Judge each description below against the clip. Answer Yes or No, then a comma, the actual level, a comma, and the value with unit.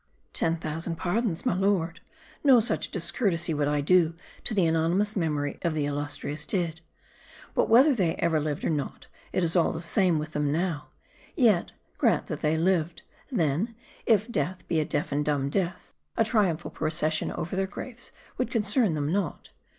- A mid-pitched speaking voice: Yes, medium, 170 Hz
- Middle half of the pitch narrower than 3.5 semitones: No, average, 4.1 semitones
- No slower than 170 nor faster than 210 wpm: Yes, average, 175 wpm